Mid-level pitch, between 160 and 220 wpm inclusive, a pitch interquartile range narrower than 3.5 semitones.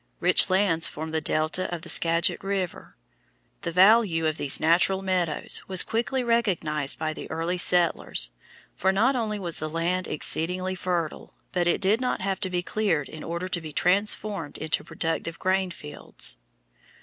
Yes: medium, 180 Hz; average, 165 wpm; average, 3.1 semitones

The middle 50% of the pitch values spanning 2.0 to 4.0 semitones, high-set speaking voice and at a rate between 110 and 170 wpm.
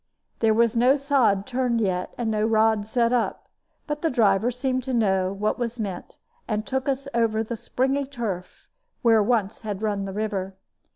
No: average, 3.3 semitones; high, 225 Hz; average, 180 wpm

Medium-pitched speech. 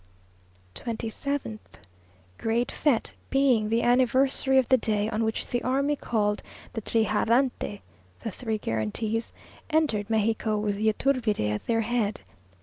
No: high, 225 Hz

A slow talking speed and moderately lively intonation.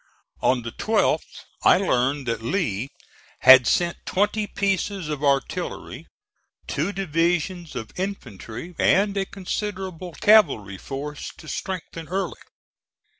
No: slow, 115 wpm; wide, 6.3 semitones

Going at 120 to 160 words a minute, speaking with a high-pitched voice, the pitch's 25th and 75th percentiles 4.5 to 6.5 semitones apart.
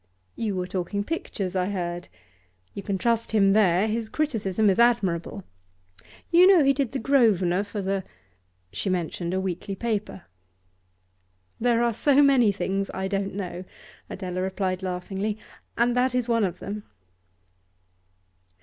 No: average, 150 wpm; high, 200 Hz; average, 4.0 semitones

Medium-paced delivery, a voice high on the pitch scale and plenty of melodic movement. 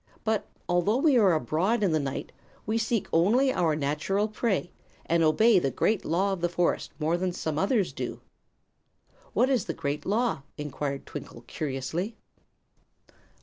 No: average, 155 wpm; medium, 175 Hz; wide, 5.7 semitones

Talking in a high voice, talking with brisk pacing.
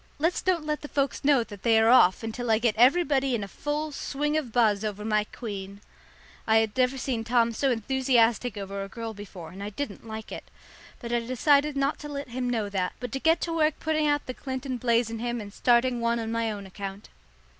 Yes: high, 235 Hz; fast, 230 wpm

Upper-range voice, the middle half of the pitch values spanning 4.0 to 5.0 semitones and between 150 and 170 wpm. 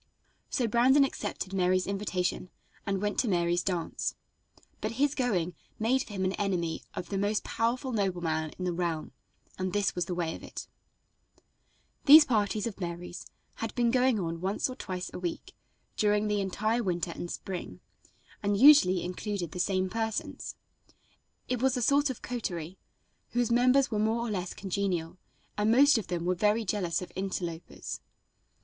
Yes: high, 200 Hz; average, 4.4 semitones; average, 165 wpm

